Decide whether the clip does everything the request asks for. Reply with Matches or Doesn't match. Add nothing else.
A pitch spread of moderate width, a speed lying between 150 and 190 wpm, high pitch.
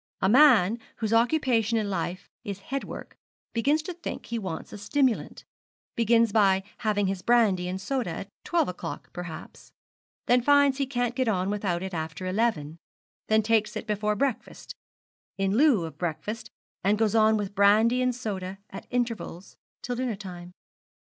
Matches